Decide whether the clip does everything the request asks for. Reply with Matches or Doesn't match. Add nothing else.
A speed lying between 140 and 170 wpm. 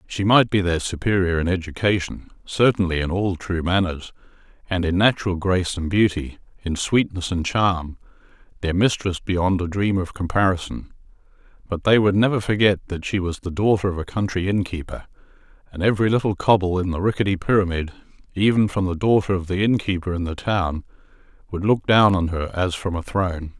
Doesn't match